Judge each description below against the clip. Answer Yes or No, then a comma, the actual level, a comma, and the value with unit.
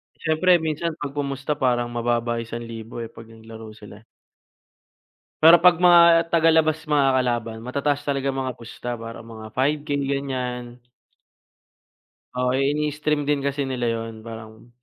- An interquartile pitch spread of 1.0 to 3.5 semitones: No, average, 4.1 semitones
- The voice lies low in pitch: Yes, low, 130 Hz